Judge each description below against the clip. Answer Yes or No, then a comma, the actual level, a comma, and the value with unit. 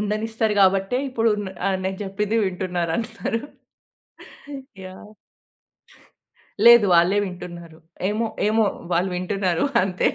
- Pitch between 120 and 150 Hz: No, high, 195 Hz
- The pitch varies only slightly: No, average, 3.2 semitones